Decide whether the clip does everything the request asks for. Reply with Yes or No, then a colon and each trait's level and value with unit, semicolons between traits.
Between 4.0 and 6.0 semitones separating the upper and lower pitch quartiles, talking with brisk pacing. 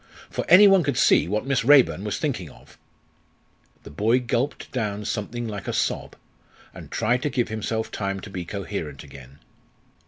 No: average, 4.3 semitones; average, 175 wpm